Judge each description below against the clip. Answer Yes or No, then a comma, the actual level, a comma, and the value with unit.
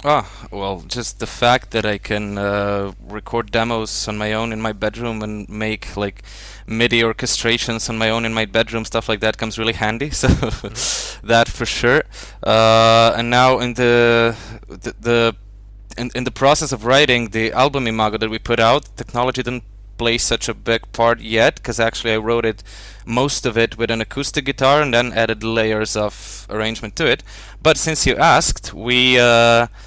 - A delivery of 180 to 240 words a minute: Yes, average, 185 wpm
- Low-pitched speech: Yes, low, 115 Hz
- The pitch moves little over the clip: Yes, narrow, 1.8 semitones